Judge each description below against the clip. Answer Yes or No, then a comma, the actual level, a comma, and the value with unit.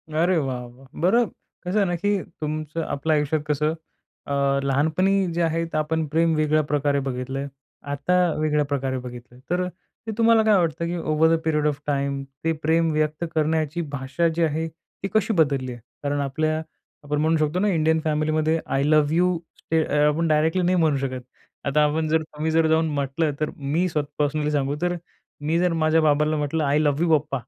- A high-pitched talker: No, medium, 155 Hz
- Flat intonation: Yes, narrow, 2.2 semitones